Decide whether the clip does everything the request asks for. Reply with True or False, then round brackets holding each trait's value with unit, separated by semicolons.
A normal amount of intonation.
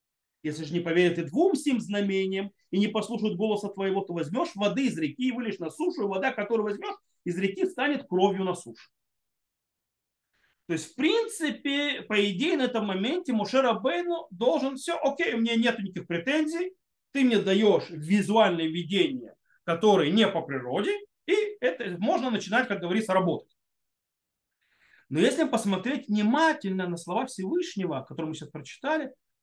False (6.9 semitones)